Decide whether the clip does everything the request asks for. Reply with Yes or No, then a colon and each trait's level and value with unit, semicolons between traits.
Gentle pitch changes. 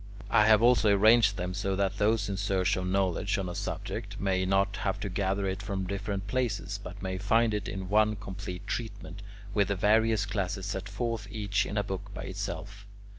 Yes: narrow, 1.7 semitones